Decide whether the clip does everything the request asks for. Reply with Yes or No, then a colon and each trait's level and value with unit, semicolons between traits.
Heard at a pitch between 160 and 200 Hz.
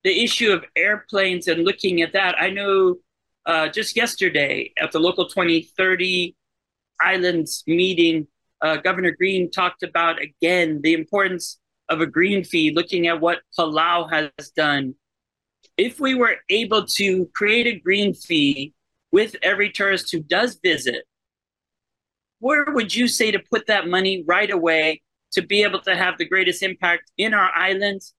Yes: medium, 185 Hz